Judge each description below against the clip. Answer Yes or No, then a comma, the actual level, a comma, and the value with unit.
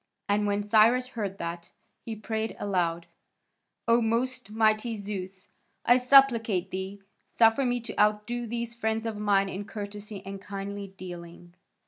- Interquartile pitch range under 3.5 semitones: Yes, average, 2.8 semitones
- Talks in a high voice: Yes, high, 210 Hz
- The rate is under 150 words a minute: Yes, average, 140 wpm